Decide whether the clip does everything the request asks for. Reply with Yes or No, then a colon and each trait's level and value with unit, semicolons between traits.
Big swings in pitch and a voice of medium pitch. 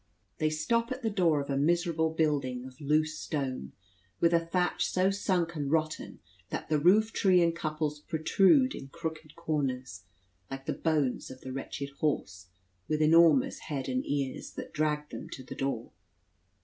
No: average, 3.4 semitones; medium, 155 Hz